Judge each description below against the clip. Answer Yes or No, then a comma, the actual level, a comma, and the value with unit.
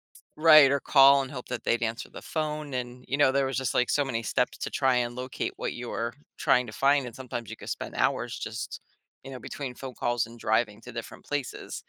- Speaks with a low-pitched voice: Yes, low, 125 Hz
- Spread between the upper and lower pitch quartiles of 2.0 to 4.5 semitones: Yes, narrow, 2.4 semitones